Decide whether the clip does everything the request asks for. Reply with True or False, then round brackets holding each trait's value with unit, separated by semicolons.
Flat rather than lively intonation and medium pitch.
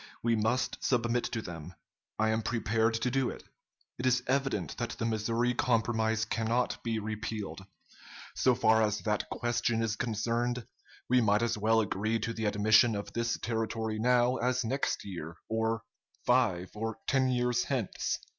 False (1.9 semitones; 115 Hz)